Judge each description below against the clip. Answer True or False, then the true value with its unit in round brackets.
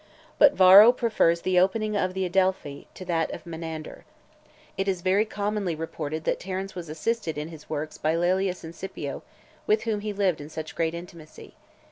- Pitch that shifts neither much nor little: True (3.4 semitones)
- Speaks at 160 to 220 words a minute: True (180 wpm)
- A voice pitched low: False (180 Hz)